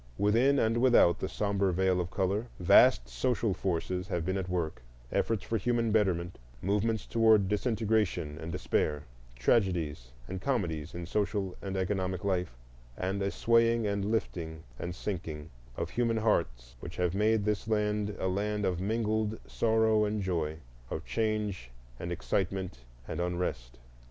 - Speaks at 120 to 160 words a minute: Yes, average, 145 wpm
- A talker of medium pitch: No, very low, 95 Hz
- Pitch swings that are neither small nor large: Yes, average, 3.8 semitones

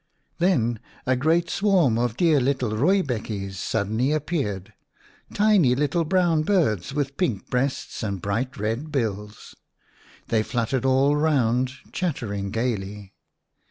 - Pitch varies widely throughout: Yes, wide, 6.0 semitones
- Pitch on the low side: Yes, low, 130 Hz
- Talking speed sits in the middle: No, slow, 125 wpm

